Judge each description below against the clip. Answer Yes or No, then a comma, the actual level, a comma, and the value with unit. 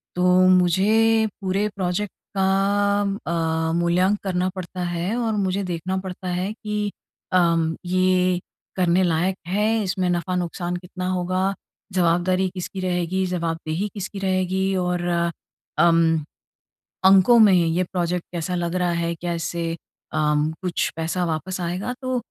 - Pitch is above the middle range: No, medium, 180 Hz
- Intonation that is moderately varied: No, narrow, 1.8 semitones